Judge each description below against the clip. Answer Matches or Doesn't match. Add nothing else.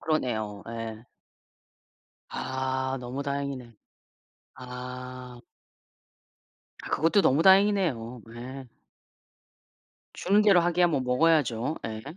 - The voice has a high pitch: Doesn't match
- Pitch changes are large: Doesn't match